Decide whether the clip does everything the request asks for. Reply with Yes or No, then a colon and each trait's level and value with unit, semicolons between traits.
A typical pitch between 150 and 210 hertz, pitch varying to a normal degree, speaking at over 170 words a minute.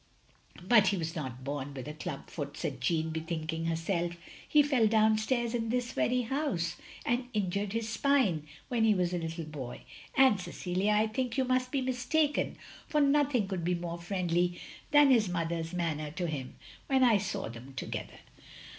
No: medium, 185 Hz; wide, 6.9 semitones; average, 185 wpm